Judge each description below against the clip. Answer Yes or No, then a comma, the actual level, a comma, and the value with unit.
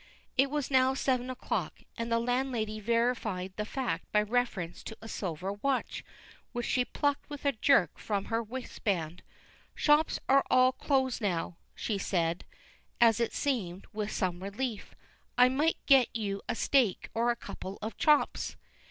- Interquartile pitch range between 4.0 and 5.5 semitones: Yes, average, 4.6 semitones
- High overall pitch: Yes, high, 230 Hz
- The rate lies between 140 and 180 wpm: Yes, average, 160 wpm